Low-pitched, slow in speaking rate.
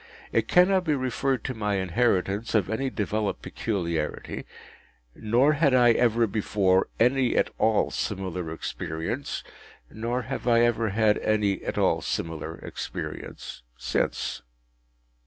Yes: low, 110 Hz; slow, 125 wpm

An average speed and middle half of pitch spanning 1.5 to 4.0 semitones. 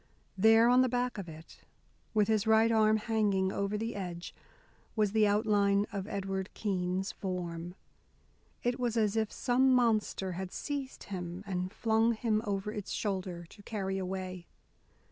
Yes: average, 155 wpm; average, 2.8 semitones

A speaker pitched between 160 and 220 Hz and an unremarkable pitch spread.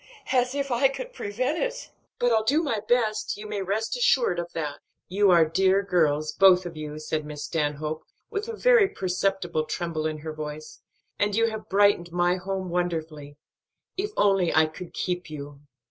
No: medium, 185 Hz; wide, 5.9 semitones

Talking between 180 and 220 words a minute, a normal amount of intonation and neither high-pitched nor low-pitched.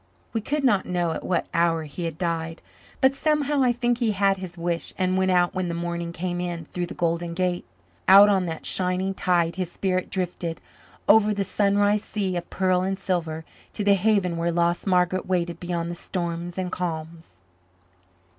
No: average, 190 wpm; narrow, 2.3 semitones; medium, 180 Hz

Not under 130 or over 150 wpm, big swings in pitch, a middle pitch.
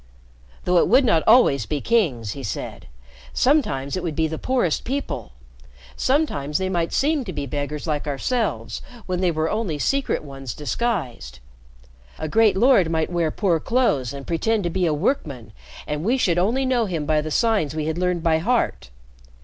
No: average, 180 wpm; wide, 7.4 semitones; medium, 170 Hz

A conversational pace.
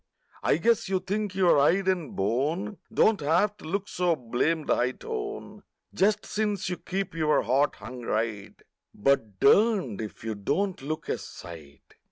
Yes: average, 160 wpm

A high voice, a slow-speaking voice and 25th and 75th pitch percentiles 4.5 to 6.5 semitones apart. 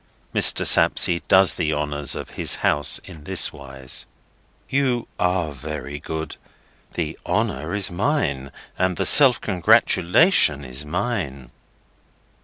No: very low, 80 Hz; slow, 120 wpm; average, 5.2 semitones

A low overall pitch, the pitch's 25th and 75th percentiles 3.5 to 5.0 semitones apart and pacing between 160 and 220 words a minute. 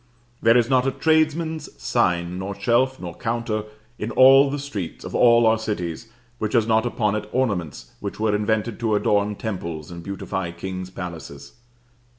Yes: low, 110 Hz; average, 4.6 semitones; average, 165 wpm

